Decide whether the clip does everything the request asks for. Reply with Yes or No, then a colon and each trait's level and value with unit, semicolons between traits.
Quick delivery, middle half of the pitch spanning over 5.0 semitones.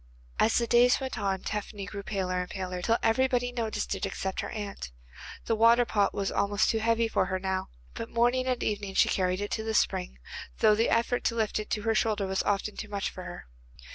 No: fast, 225 wpm; average, 3.0 semitones